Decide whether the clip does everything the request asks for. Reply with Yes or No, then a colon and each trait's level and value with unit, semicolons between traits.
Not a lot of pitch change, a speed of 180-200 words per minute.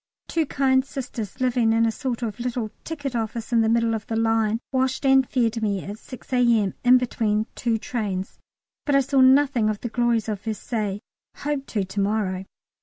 No: average, 3.2 semitones; average, 190 wpm